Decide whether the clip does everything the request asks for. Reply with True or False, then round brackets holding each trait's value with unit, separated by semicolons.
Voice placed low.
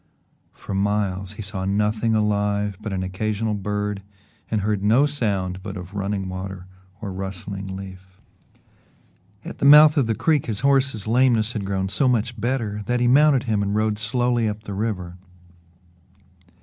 True (105 Hz)